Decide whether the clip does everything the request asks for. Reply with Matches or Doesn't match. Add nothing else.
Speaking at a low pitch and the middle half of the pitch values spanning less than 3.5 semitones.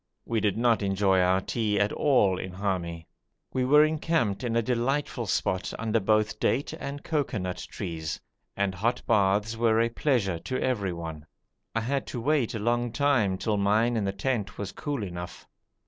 Doesn't match